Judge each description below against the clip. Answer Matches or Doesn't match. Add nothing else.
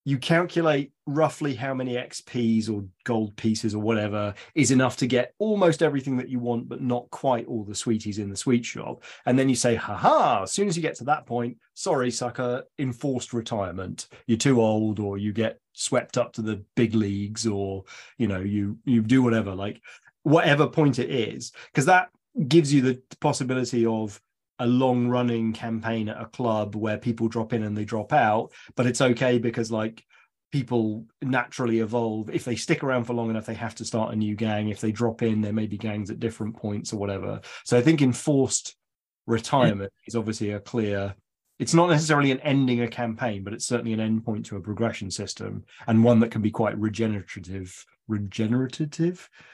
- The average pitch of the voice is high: Doesn't match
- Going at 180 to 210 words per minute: Matches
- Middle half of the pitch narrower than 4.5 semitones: Matches